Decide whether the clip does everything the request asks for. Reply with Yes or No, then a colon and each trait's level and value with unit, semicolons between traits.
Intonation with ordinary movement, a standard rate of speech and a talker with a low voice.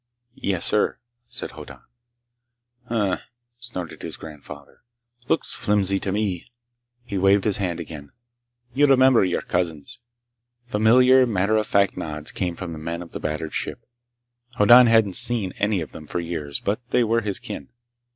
Yes: average, 4.9 semitones; average, 160 wpm; low, 100 Hz